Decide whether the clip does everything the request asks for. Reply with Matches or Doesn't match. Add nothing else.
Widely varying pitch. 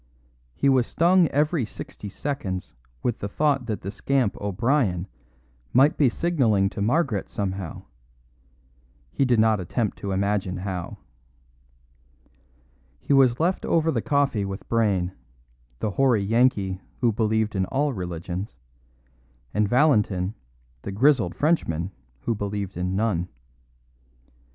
Matches